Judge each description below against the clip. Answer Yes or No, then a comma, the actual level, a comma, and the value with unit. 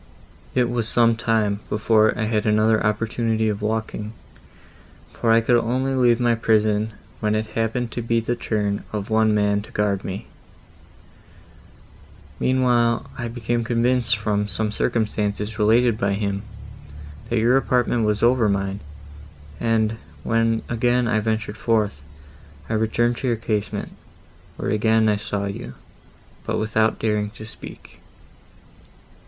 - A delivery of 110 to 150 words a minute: Yes, average, 140 wpm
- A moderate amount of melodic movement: No, narrow, 1.8 semitones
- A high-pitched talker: No, low, 110 Hz